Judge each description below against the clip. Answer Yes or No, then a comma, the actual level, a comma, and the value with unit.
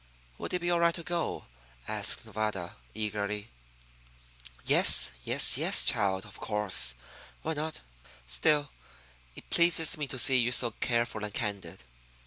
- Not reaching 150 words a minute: Yes, average, 140 wpm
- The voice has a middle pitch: No, low, 110 Hz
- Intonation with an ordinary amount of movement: No, wide, 7.0 semitones